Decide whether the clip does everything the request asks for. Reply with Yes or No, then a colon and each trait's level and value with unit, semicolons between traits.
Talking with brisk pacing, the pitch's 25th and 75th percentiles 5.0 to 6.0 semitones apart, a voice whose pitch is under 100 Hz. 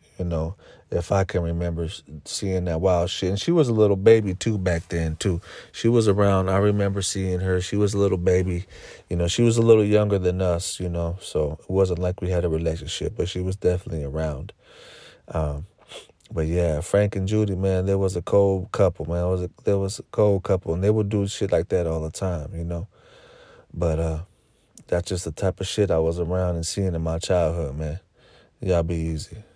No: fast, 220 wpm; average, 3.0 semitones; very low, 90 Hz